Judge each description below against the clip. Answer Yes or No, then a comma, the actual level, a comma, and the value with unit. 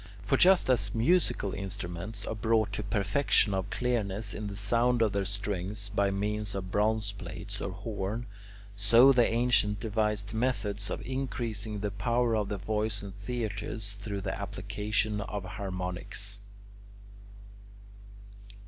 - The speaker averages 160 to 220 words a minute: No, average, 145 wpm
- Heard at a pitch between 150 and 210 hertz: No, low, 105 Hz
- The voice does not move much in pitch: Yes, narrow, 2.0 semitones